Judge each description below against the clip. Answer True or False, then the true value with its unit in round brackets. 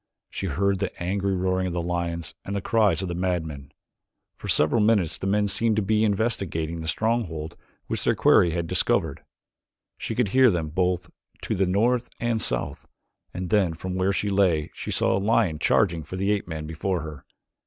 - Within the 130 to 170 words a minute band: False (195 wpm)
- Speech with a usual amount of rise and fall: True (3.6 semitones)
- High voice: False (95 Hz)